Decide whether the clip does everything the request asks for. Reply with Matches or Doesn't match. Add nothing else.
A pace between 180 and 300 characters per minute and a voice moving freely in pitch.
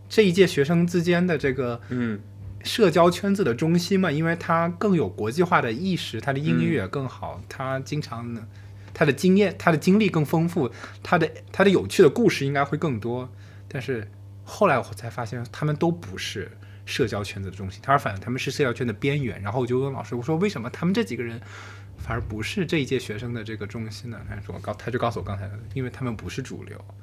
Doesn't match